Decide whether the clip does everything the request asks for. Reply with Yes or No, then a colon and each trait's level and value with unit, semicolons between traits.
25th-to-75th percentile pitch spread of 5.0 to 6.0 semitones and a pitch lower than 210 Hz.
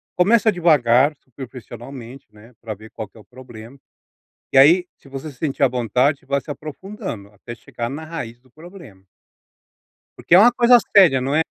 Yes: average, 5.3 semitones; low, 135 Hz